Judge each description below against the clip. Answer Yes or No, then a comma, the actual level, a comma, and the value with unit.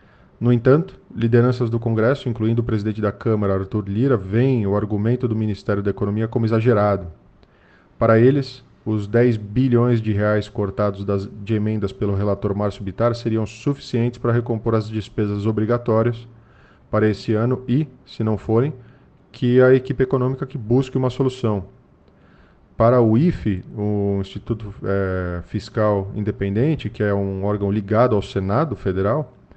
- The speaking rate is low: No, average, 150 wpm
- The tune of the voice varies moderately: Yes, average, 3.0 semitones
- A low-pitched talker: Yes, low, 110 Hz